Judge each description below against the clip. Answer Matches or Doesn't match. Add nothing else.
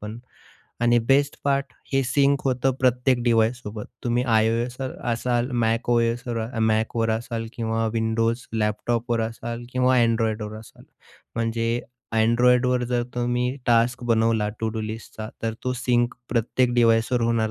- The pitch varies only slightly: Matches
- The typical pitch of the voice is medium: Doesn't match